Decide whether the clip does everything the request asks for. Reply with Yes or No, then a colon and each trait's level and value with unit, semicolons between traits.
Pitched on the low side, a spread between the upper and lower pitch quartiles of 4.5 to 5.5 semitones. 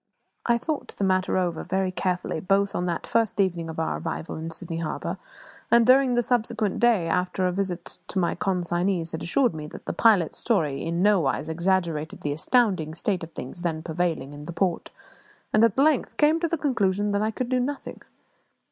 No: medium, 185 Hz; average, 5.1 semitones